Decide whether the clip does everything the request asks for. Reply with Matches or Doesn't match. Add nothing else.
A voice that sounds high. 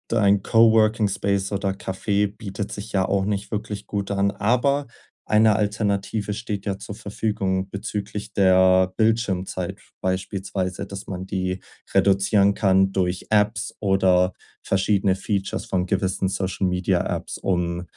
Doesn't match